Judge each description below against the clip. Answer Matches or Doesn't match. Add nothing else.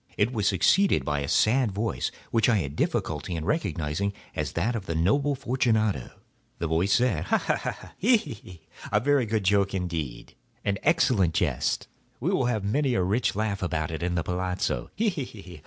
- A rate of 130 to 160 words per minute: Doesn't match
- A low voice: Matches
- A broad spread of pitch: Matches